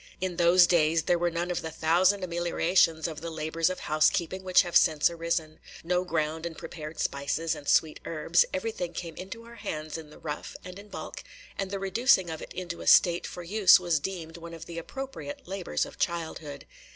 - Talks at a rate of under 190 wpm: No, fast, 205 wpm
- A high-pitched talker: No, medium, 170 Hz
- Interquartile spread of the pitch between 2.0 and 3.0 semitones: Yes, narrow, 2.4 semitones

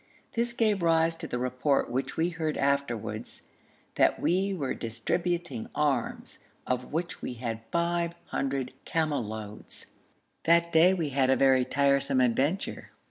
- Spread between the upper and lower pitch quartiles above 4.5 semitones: Yes, average, 5.0 semitones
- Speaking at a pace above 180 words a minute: No, average, 140 wpm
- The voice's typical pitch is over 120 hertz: Yes, medium, 140 Hz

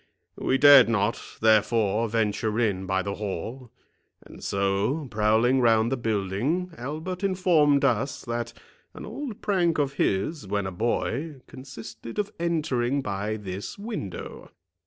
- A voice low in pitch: Yes, low, 120 Hz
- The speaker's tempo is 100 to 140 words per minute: Yes, slow, 135 wpm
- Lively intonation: Yes, wide, 5.8 semitones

